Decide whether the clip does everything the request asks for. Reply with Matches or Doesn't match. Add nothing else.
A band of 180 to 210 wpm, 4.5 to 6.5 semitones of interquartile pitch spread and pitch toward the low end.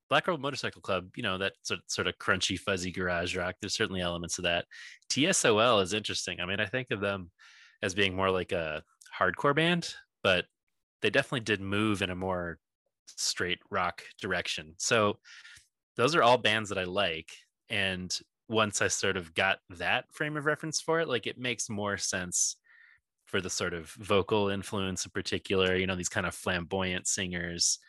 Doesn't match